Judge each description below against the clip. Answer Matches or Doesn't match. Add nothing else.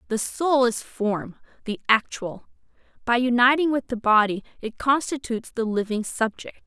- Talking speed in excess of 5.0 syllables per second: Doesn't match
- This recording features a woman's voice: Matches